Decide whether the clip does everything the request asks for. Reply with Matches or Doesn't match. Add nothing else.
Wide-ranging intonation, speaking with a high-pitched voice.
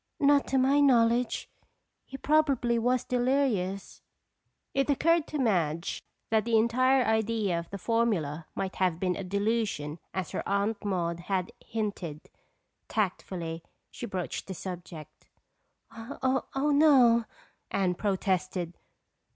Matches